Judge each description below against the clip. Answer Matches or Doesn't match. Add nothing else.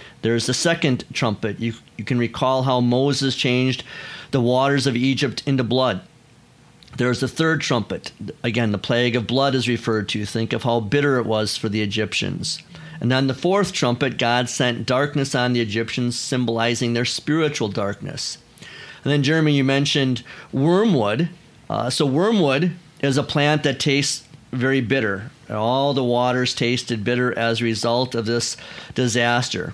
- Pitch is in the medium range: Doesn't match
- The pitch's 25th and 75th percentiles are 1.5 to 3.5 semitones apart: Matches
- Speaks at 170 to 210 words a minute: Doesn't match